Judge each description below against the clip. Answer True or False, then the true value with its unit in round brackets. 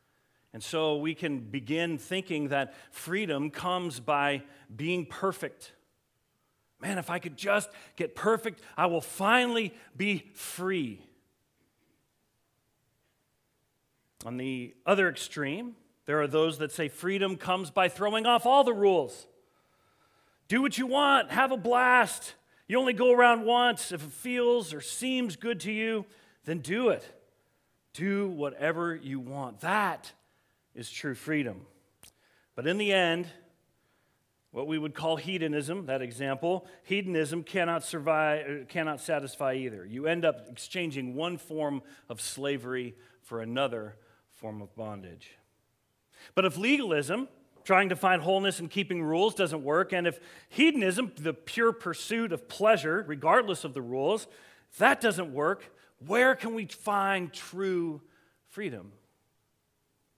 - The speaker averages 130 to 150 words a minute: True (135 wpm)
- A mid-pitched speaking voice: True (170 Hz)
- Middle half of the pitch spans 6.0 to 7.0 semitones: True (6.4 semitones)